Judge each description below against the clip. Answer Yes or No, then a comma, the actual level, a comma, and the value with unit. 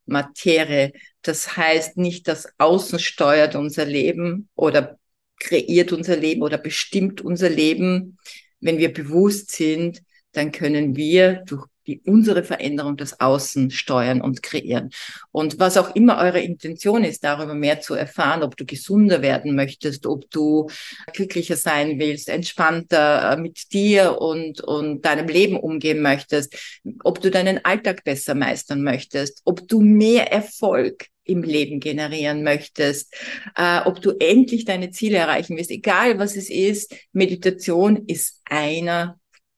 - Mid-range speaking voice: Yes, medium, 165 Hz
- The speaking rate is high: No, average, 140 wpm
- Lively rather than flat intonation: No, average, 4.0 semitones